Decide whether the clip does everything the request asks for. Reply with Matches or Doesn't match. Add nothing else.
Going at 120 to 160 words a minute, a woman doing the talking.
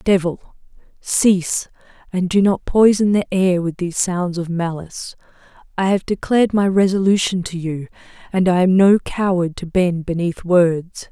Matches